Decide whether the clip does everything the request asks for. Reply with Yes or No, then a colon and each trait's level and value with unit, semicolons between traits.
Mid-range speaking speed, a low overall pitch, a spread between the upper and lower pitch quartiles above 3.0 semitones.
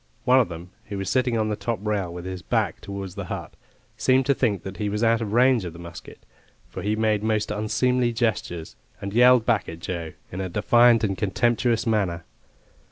No: fast, 210 wpm; low, 105 Hz; average, 4.1 semitones